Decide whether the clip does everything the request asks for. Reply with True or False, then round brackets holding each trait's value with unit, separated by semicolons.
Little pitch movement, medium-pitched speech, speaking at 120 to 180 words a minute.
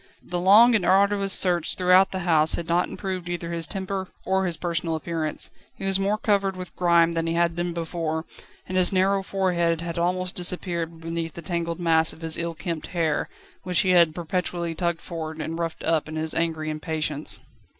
False (2.0 semitones; 170 Hz; 195 wpm)